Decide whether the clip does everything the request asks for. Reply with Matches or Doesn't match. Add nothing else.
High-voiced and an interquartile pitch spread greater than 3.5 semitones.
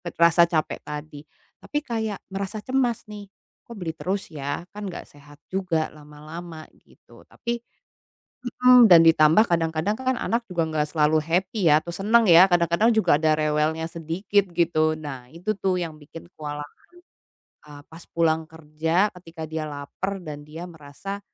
Doesn't match